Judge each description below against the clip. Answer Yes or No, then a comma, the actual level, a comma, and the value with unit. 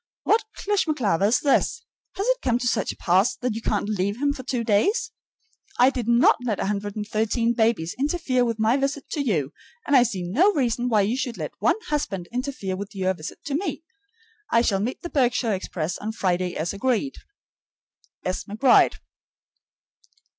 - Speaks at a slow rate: No, average, 175 wpm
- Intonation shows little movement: No, average, 5.0 semitones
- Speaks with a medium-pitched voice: No, high, 235 Hz